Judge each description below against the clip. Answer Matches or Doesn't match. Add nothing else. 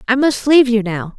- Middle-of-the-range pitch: Doesn't match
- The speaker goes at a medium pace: Doesn't match